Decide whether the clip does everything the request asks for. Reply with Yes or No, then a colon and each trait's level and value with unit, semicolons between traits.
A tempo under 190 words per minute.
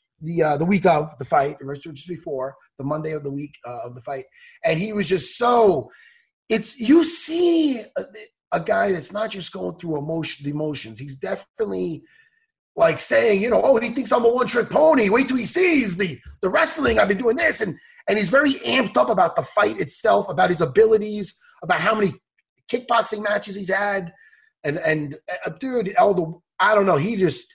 No: fast, 205 wpm